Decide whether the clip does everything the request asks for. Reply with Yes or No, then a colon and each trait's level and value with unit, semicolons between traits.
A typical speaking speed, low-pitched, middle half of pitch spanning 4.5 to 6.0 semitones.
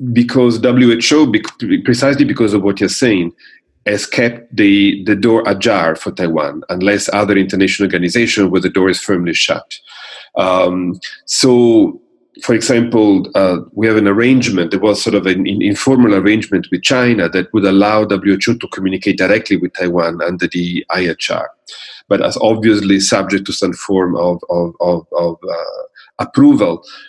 Yes: average, 155 wpm; low, 105 Hz; average, 4.8 semitones